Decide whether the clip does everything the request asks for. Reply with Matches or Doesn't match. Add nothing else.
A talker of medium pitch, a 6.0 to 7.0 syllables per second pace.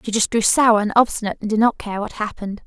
Doesn't match